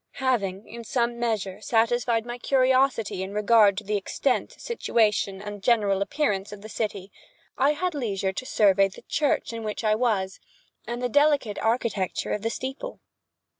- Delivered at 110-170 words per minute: Yes, average, 165 wpm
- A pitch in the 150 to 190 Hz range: No, high, 225 Hz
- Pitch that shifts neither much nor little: Yes, average, 3.7 semitones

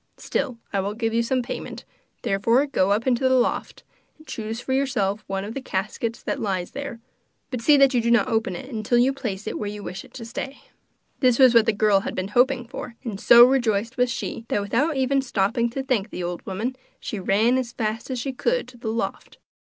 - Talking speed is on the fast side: Yes, fast, 230 wpm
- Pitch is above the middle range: Yes, high, 235 Hz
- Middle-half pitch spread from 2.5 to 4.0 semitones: Yes, average, 3.7 semitones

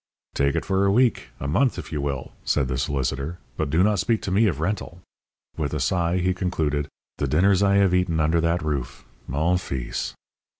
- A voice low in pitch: Yes, very low, 85 Hz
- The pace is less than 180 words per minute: No, fast, 205 wpm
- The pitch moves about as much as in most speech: Yes, average, 5.0 semitones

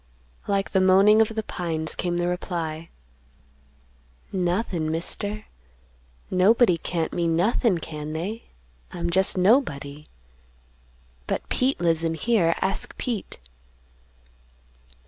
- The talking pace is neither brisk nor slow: No, slow, 105 wpm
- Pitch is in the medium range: Yes, medium, 180 Hz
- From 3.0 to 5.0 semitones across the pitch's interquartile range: Yes, average, 3.9 semitones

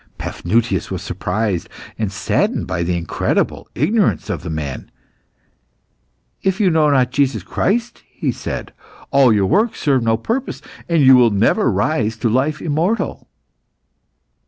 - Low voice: Yes, low, 125 Hz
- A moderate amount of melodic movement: No, wide, 7.4 semitones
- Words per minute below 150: Yes, average, 140 wpm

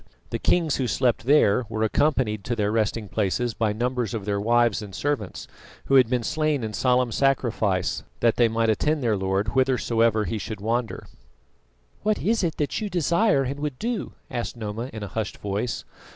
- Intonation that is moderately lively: Yes, average, 4.2 semitones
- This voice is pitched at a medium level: No, low, 115 Hz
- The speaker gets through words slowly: No, average, 180 wpm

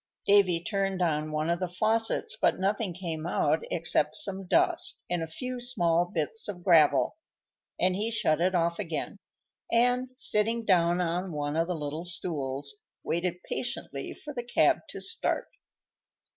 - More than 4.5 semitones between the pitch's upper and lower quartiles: No, average, 4.1 semitones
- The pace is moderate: Yes, average, 160 wpm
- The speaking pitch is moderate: Yes, medium, 180 Hz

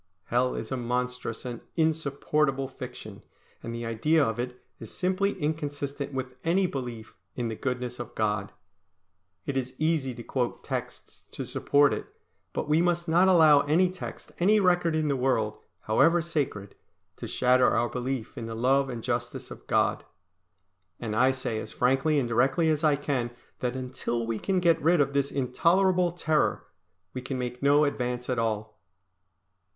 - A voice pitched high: No, low, 135 Hz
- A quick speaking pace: No, average, 170 wpm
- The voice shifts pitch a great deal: No, average, 4.3 semitones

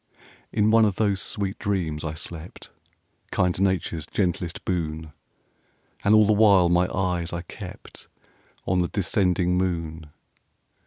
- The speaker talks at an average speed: No, slow, 130 wpm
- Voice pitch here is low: Yes, very low, 90 Hz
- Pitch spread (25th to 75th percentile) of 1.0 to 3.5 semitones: Yes, average, 2.8 semitones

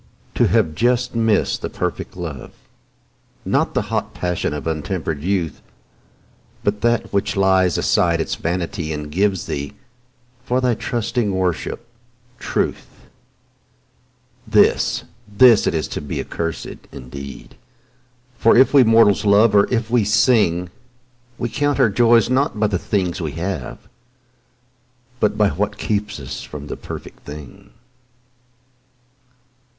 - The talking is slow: Yes, slow, 130 wpm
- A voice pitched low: Yes, low, 100 Hz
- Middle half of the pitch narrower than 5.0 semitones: No, wide, 5.6 semitones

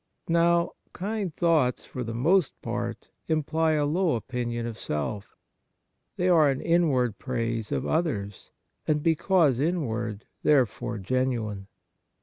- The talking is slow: Yes, slow, 130 wpm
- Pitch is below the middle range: Yes, low, 130 Hz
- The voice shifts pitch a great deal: Yes, wide, 6.1 semitones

